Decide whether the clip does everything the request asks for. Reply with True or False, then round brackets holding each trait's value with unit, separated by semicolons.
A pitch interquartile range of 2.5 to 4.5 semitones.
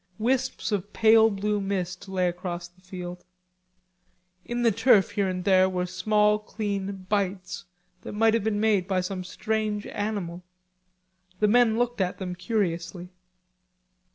True (3.0 semitones)